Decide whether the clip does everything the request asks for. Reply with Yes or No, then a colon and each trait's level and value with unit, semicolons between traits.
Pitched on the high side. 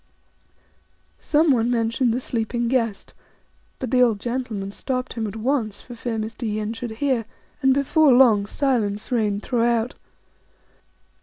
Yes: high, 235 Hz